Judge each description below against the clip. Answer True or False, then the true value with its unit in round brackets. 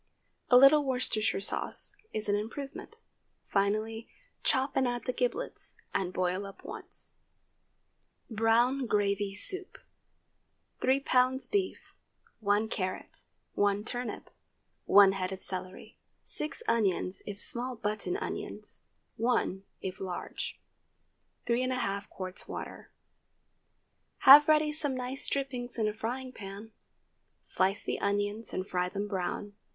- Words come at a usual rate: False (115 wpm)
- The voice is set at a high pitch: True (220 Hz)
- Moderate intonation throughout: True (4.5 semitones)